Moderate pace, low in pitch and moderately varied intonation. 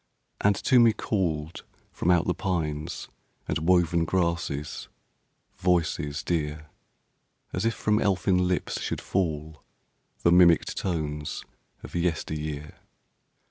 No: slow, 110 wpm; very low, 85 Hz; average, 3.1 semitones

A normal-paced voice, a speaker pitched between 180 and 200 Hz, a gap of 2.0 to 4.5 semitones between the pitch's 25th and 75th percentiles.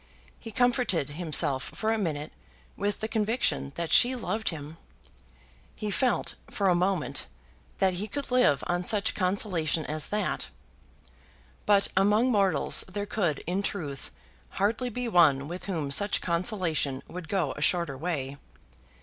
No: average, 145 wpm; medium, 185 Hz; average, 5.2 semitones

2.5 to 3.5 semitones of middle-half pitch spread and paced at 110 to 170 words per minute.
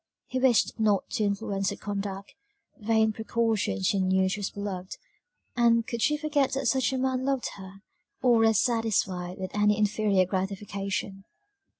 Yes: average, 3.1 semitones; average, 160 wpm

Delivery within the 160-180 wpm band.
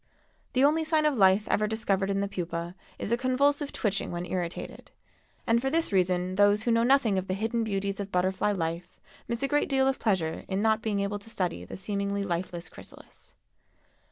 No: average, 200 wpm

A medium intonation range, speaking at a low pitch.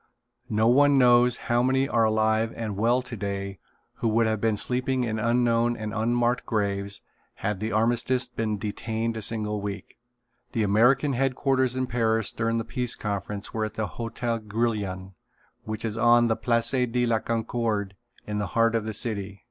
No: narrow, 2.2 semitones; low, 115 Hz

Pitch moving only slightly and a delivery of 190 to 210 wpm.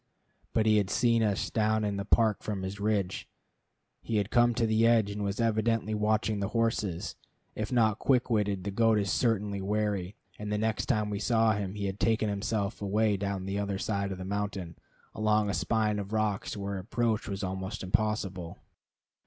Yes: narrow, 1.8 semitones; average, 195 wpm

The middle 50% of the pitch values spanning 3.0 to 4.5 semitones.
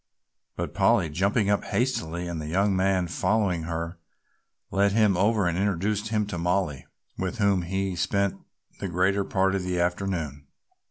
No: narrow, 2.5 semitones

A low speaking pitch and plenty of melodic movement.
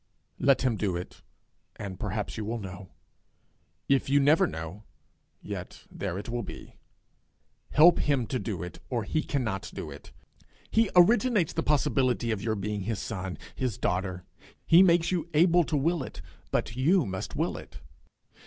Yes: low, 120 Hz; wide, 7.8 semitones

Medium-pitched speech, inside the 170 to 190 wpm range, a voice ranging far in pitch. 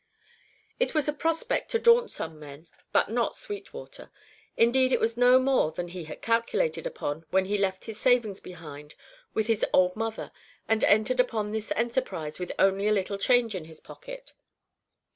No: high, 220 Hz; average, 175 wpm; wide, 5.7 semitones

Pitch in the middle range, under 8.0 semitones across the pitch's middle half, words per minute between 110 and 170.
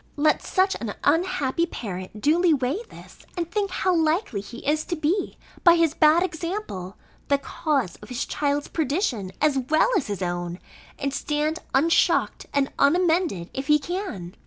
No: very high, 300 Hz; wide, 5.4 semitones; average, 160 wpm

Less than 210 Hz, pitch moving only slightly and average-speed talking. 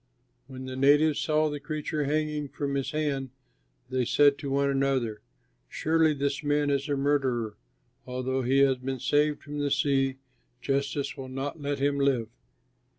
Yes: medium, 140 Hz; narrow, 1.6 semitones; average, 160 wpm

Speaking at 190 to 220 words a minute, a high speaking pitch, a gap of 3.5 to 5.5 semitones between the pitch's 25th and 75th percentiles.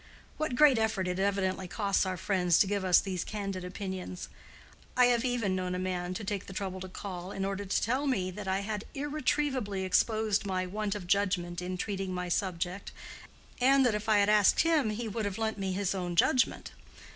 No: fast, 205 wpm; high, 195 Hz; average, 2.8 semitones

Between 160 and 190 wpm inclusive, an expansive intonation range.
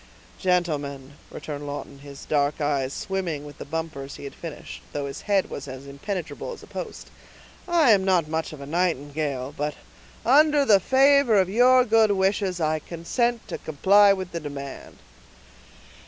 Yes: average, 165 wpm; wide, 6.0 semitones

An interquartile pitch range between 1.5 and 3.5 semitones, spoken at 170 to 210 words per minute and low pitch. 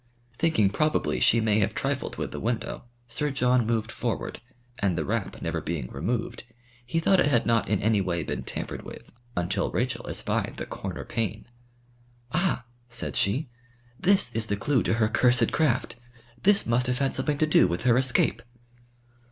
No: average, 4.0 semitones; average, 175 wpm; low, 120 Hz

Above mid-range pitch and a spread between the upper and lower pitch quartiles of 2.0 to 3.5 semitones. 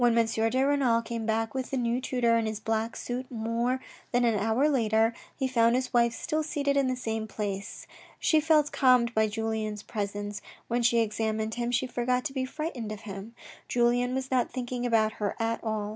Yes: high, 235 Hz; narrow, 2.5 semitones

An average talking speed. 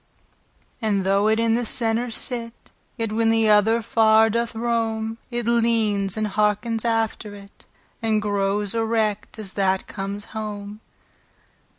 No: slow, 130 wpm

